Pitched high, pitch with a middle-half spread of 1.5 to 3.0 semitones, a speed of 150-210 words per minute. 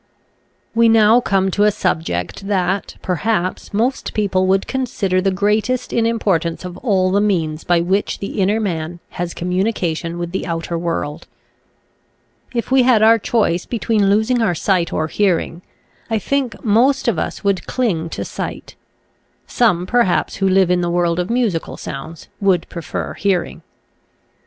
No: high, 195 Hz; average, 4.3 semitones; average, 160 wpm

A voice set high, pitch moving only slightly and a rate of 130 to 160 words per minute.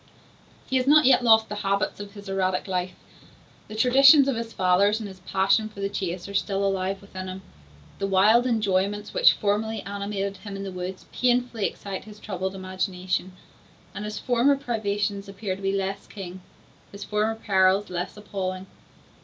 No: high, 200 Hz; narrow, 2.3 semitones; average, 175 wpm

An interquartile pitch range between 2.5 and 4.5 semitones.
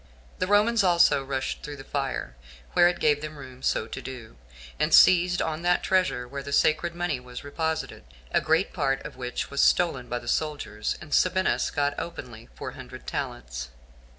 No: average, 5.2 semitones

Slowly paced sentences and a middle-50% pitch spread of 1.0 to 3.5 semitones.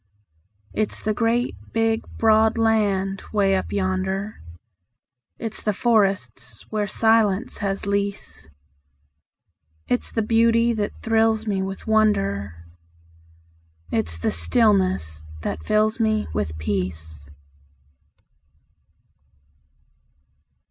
Yes: slow, 95 wpm; average, 3.0 semitones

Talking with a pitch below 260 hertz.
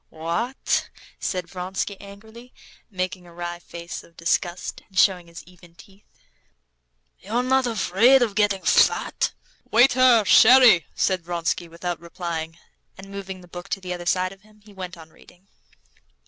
Yes: medium, 185 Hz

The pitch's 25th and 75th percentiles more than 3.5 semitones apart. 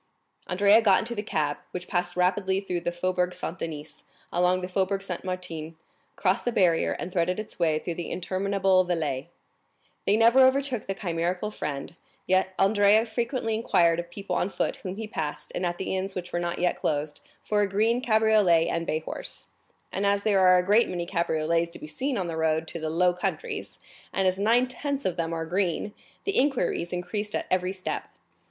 No: average, 3.2 semitones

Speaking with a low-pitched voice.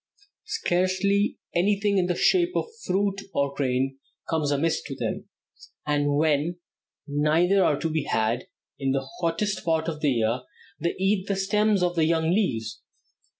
No: medium, 165 Hz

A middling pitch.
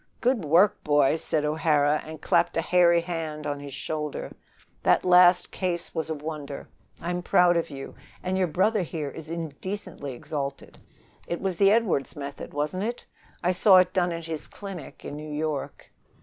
Yes: medium, 165 Hz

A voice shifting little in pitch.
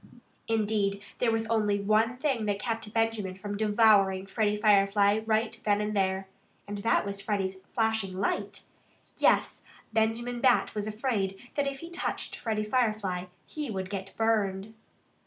Yes: narrow, 2.1 semitones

